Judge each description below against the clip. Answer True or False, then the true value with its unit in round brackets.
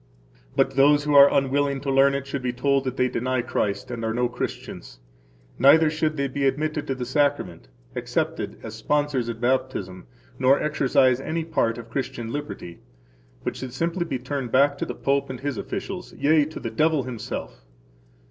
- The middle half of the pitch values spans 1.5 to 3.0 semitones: True (2.7 semitones)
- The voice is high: False (135 Hz)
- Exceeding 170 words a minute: True (185 wpm)